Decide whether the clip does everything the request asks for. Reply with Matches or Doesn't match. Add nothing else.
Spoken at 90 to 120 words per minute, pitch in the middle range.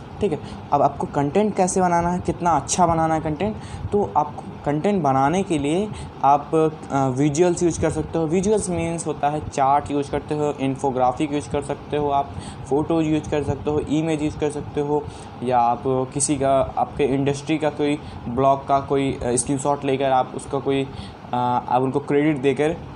Doesn't match